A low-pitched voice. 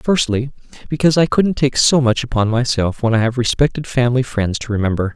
Yes: low, 125 Hz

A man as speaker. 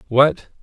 Yes: male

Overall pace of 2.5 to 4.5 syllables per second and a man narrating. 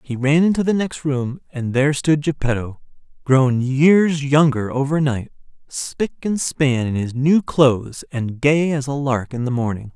Yes: 4.4 syllables/s; male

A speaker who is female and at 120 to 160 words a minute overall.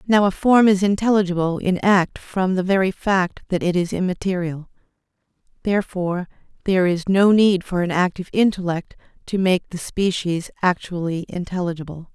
Yes: female; average, 150 wpm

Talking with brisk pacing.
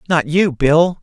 No: average, 175 wpm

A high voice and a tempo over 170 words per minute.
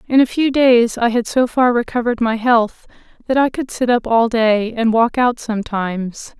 Yes: high, 235 Hz; fast, 205 wpm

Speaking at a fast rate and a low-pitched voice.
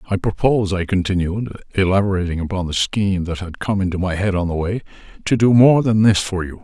Yes: fast, 215 wpm; very low, 95 Hz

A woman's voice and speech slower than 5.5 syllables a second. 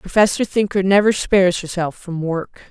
Yes: female; 5.0 syllables/s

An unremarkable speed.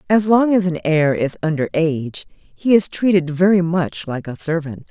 Yes: average, 195 wpm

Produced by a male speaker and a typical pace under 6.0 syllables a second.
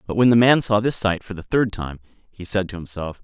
Yes: male; 5.5 syllables/s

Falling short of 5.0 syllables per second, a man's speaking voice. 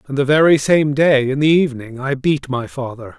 No: 5.3 syllables/s; male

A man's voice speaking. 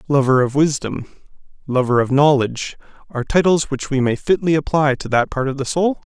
Yes: male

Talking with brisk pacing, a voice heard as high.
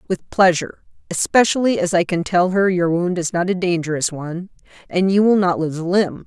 No: fast, 210 wpm; medium, 180 Hz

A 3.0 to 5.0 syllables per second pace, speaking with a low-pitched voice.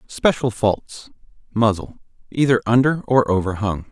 Yes: 4.4 syllables/s; low, 115 Hz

